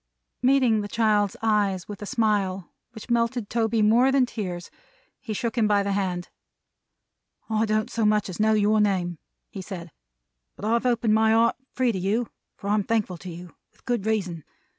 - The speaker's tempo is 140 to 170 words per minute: No, average, 185 wpm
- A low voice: No, high, 215 Hz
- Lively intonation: No, average, 2.7 semitones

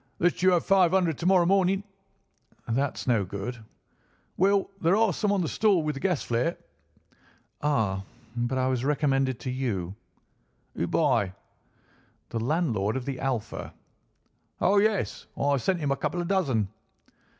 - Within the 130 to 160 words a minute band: Yes, average, 155 wpm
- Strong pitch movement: Yes, wide, 7.0 semitones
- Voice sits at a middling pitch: Yes, medium, 145 Hz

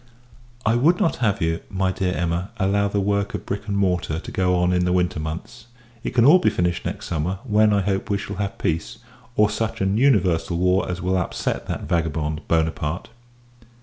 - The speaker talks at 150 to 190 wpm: No, fast, 205 wpm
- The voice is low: Yes, very low, 95 Hz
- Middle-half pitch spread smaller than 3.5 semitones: Yes, average, 2.9 semitones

